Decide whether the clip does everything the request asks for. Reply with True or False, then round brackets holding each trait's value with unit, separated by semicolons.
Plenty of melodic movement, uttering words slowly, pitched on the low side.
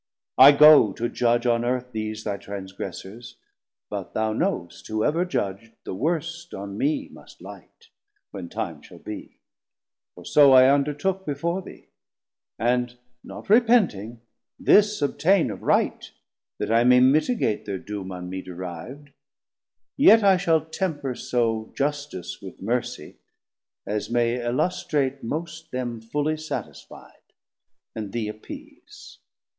True (6.2 semitones; 130 wpm; 125 Hz)